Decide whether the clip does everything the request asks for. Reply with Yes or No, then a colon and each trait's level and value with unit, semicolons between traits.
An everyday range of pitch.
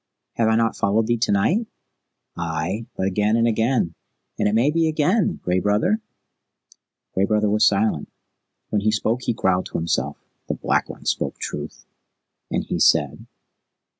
Yes: average, 3.2 semitones